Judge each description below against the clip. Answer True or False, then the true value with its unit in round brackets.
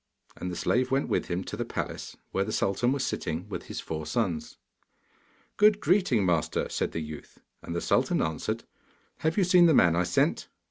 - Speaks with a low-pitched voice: True (95 Hz)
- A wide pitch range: True (8.6 semitones)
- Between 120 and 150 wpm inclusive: False (195 wpm)